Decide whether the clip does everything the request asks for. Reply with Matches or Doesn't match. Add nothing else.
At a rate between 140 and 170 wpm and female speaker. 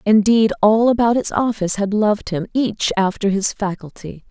Matches